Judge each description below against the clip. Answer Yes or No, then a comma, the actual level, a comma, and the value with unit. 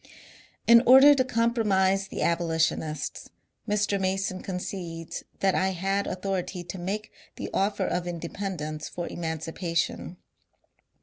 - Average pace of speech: No, slow, 120 wpm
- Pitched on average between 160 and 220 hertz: Yes, high, 190 Hz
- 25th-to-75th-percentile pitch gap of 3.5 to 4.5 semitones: No, average, 2.9 semitones